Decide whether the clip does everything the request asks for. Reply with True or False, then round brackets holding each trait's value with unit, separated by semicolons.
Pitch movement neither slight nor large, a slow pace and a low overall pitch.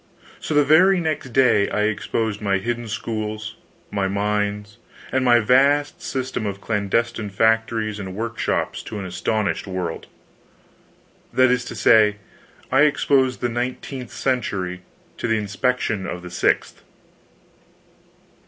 True (3.6 semitones; 130 wpm; 110 Hz)